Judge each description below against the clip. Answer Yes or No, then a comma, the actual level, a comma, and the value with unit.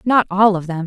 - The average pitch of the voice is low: No, high, 195 Hz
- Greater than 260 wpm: Yes, fast, 280 wpm